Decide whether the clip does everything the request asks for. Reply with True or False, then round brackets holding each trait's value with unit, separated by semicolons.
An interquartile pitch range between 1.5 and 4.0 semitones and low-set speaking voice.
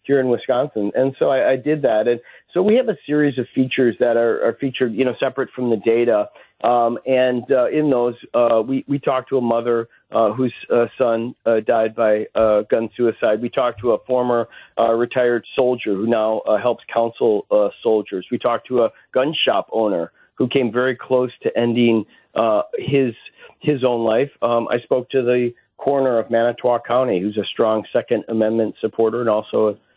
True (2.4 semitones; 120 Hz)